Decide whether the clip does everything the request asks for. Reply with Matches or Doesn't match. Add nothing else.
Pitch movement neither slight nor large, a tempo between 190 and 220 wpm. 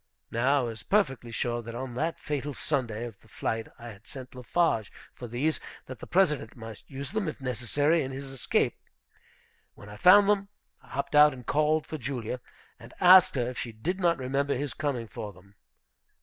Matches